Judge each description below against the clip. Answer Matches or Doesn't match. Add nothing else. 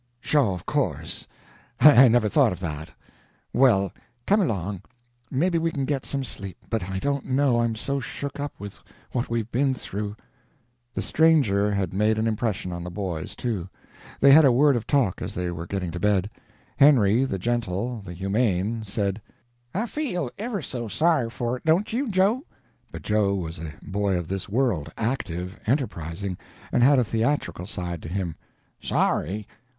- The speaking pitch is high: Doesn't match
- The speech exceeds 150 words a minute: Matches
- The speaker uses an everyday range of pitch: Doesn't match